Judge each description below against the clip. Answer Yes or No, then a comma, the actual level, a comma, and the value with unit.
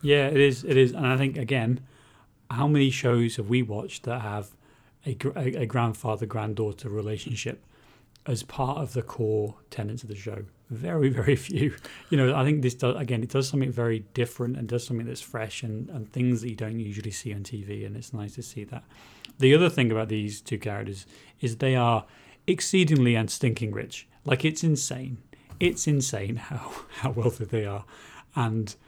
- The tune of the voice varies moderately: Yes, average, 3.3 semitones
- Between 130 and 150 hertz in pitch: No, low, 120 Hz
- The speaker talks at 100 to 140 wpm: No, average, 190 wpm